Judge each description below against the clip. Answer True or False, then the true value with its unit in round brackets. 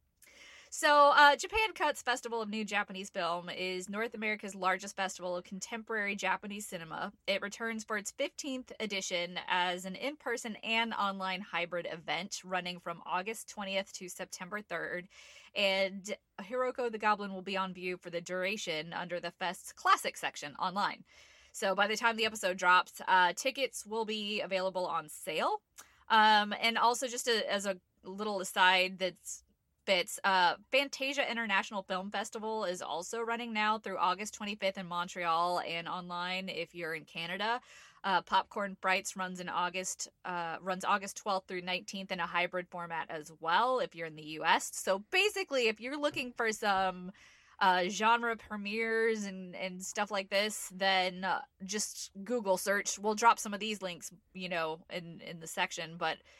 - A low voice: False (195 Hz)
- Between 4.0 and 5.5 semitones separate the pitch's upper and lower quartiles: False (3.5 semitones)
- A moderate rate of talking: True (165 wpm)